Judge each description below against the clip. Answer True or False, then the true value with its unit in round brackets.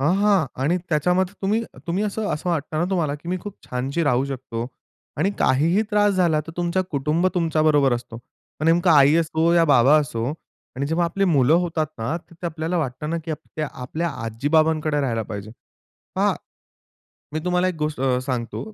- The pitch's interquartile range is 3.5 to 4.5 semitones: True (4.0 semitones)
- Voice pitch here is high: False (155 Hz)